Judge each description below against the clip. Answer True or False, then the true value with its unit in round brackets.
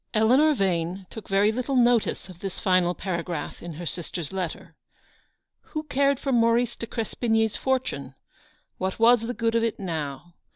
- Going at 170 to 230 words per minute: False (160 wpm)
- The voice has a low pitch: False (215 Hz)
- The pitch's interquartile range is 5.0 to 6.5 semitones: True (5.4 semitones)